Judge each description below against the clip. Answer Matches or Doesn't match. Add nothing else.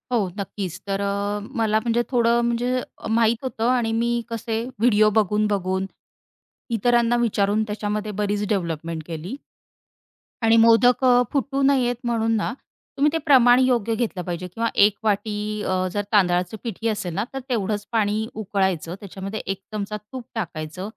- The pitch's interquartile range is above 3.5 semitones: Doesn't match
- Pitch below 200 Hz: Doesn't match